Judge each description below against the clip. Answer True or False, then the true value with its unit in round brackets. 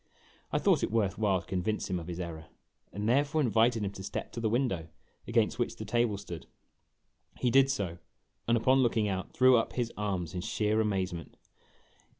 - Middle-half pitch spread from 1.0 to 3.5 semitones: False (4.2 semitones)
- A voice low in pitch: True (105 Hz)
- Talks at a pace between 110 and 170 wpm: False (195 wpm)